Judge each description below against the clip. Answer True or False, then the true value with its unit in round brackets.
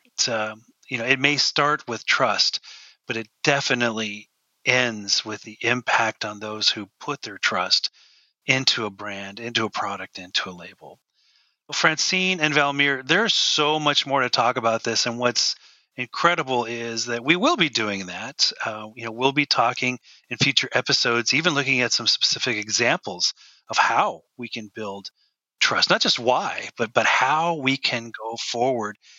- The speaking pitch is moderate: False (120 Hz)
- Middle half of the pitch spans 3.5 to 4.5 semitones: True (3.9 semitones)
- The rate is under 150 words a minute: False (170 wpm)